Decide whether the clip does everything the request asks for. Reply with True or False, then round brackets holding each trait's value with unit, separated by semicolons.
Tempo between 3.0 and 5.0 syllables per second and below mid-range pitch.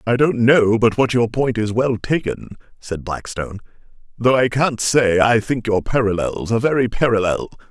True (4.9 syllables/s; 115 Hz)